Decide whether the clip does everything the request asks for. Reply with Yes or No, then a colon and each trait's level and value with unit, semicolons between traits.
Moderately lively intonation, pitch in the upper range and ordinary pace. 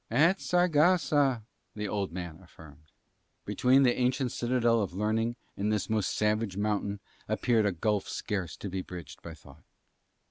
No: average, 4.7 semitones; low, 105 Hz; average, 150 wpm